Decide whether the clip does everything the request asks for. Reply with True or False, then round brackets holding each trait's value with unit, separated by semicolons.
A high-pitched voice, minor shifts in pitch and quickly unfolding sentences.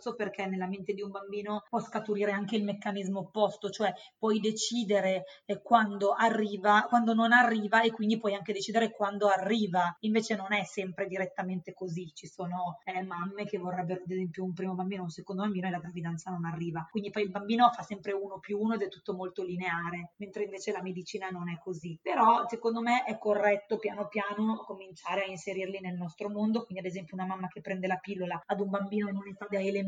True (200 Hz; 2.1 semitones; 205 wpm)